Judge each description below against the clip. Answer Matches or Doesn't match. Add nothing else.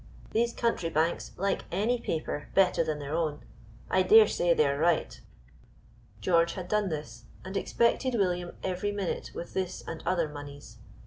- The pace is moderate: Matches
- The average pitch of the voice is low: Doesn't match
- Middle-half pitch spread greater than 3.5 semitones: Matches